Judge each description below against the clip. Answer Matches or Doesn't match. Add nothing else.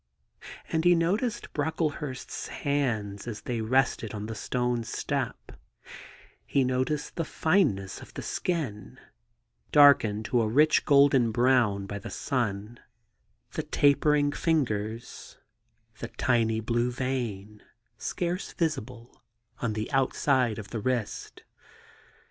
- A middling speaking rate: Doesn't match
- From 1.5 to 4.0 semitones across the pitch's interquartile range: Doesn't match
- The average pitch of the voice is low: Matches